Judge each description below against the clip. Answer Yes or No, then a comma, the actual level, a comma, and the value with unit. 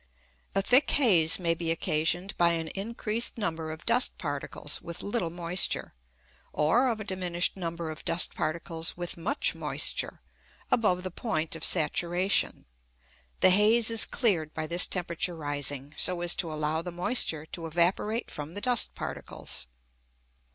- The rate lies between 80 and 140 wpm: No, average, 150 wpm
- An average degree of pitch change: Yes, average, 3.7 semitones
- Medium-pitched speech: Yes, medium, 175 Hz